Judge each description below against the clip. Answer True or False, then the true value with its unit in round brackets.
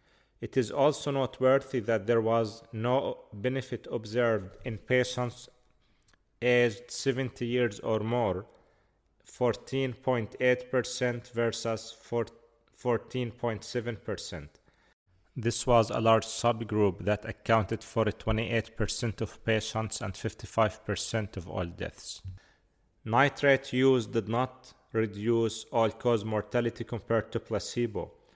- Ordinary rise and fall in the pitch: False (2.0 semitones)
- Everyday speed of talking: False (100 wpm)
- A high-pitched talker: False (115 Hz)